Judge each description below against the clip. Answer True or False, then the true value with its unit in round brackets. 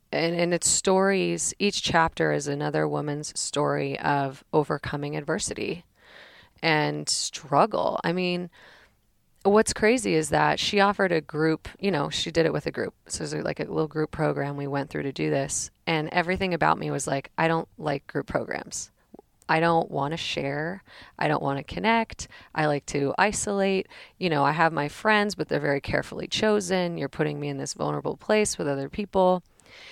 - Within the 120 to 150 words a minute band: False (185 wpm)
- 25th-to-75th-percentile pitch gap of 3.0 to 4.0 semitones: False (4.6 semitones)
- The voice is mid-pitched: True (160 Hz)